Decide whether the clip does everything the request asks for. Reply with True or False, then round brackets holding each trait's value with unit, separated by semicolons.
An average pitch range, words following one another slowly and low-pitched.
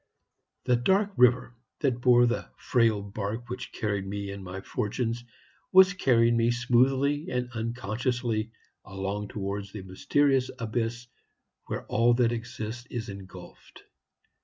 True (3.2 semitones; 130 wpm; 120 Hz)